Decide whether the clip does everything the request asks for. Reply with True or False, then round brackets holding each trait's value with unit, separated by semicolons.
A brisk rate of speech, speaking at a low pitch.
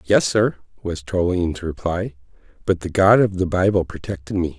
False (170 wpm; 90 Hz)